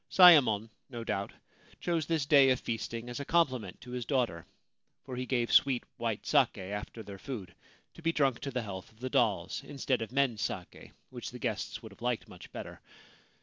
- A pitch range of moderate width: Yes, average, 3.8 semitones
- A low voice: Yes, low, 125 Hz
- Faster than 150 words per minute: Yes, average, 200 wpm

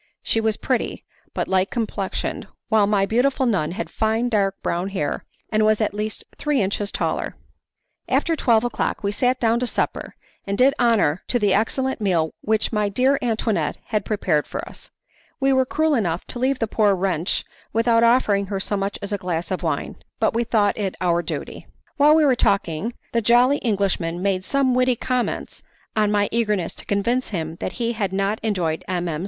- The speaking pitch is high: Yes, high, 215 Hz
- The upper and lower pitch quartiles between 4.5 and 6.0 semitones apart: No, average, 3.7 semitones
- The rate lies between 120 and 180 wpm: No, average, 195 wpm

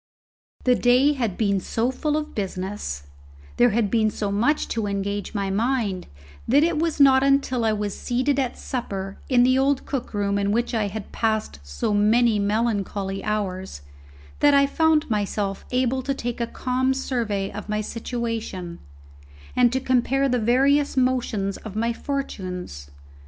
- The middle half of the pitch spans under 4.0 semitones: No, average, 4.4 semitones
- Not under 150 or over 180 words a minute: Yes, average, 160 wpm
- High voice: Yes, high, 230 Hz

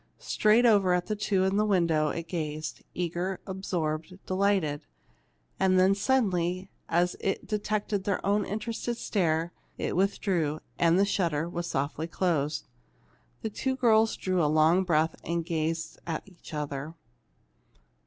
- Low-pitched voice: No, medium, 180 Hz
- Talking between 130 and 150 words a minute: Yes, average, 145 wpm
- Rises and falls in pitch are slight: No, average, 3.7 semitones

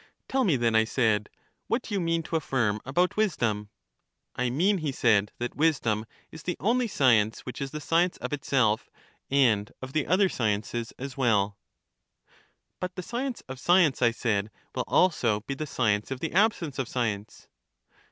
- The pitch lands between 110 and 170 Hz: Yes, low, 135 Hz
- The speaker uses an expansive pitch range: Yes, wide, 7.0 semitones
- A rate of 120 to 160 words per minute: No, average, 170 wpm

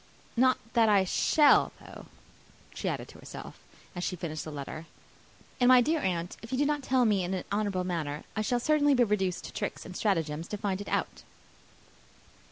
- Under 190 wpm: No, average, 195 wpm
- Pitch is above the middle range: Yes, high, 205 Hz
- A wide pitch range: Yes, wide, 5.9 semitones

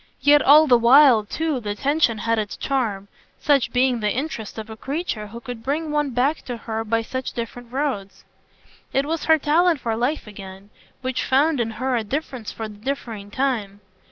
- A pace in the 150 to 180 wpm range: No, average, 190 wpm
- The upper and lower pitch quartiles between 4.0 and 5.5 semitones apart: Yes, average, 4.4 semitones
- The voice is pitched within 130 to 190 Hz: No, high, 245 Hz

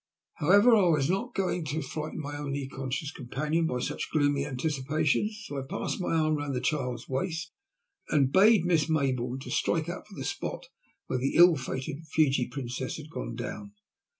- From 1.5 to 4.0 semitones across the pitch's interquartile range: Yes, average, 3.7 semitones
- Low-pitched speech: No, medium, 145 Hz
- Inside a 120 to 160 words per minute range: No, average, 180 wpm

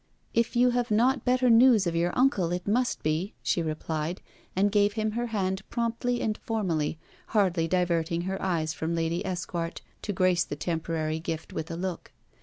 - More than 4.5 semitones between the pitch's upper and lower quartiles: Yes, average, 5.1 semitones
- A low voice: No, medium, 185 Hz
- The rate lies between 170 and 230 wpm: Yes, average, 180 wpm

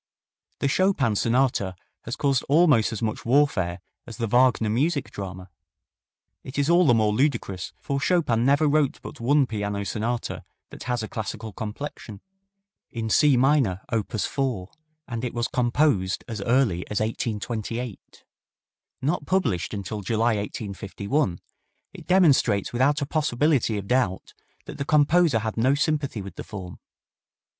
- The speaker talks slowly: No, average, 145 wpm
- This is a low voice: Yes, low, 120 Hz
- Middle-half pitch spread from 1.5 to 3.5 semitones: No, average, 5.1 semitones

